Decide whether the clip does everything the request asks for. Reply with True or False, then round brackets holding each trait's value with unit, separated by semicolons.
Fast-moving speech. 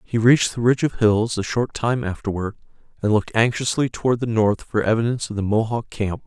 True (210 wpm)